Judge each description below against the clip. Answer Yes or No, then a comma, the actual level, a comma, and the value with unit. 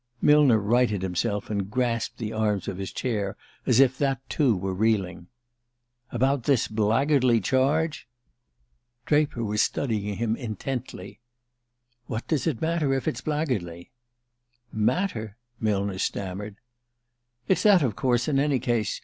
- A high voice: No, low, 115 Hz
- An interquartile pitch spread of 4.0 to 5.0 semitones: Yes, average, 4.7 semitones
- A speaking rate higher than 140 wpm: No, slow, 135 wpm